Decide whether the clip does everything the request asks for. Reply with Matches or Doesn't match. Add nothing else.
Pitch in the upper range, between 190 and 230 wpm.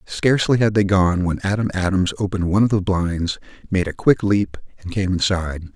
Doesn't match